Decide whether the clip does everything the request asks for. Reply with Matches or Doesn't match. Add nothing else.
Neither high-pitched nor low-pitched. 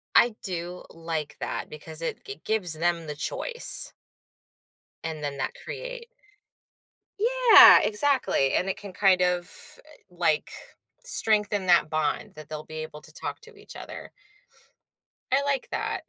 Matches